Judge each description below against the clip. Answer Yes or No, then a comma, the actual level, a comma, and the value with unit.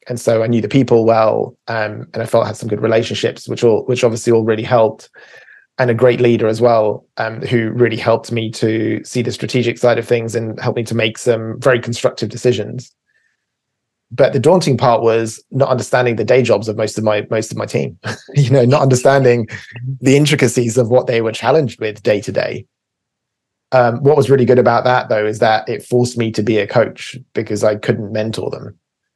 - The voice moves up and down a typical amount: No, narrow, 2.1 semitones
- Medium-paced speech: No, fast, 215 wpm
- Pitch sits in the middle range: No, low, 115 Hz